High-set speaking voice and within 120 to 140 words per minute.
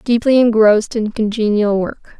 Yes: high, 220 Hz; slow, 135 wpm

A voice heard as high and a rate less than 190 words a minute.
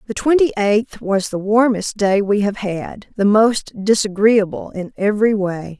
Yes: high, 205 Hz; average, 165 wpm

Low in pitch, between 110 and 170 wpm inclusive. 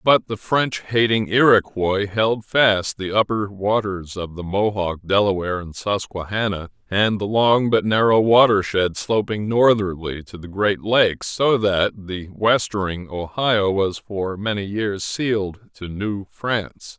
Yes: low, 100 Hz; average, 145 wpm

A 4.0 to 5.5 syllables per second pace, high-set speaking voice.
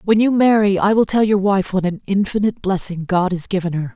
No: 5.9 syllables/s; high, 195 Hz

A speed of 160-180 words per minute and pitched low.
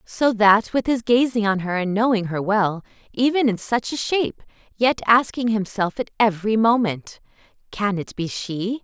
No: average, 175 wpm; high, 220 Hz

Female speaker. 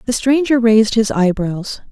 Yes: female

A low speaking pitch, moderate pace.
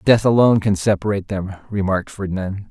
Yes: low, 100 Hz; average, 155 wpm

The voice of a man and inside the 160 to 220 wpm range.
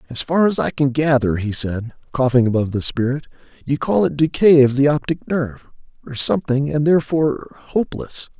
Yes: male; average, 180 wpm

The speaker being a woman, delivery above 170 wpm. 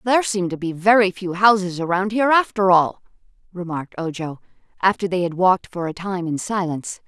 Yes: female; average, 185 wpm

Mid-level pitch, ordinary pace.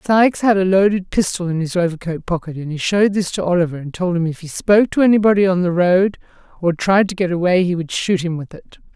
No: medium, 180 Hz; fast, 250 wpm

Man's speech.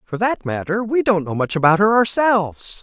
Yes: male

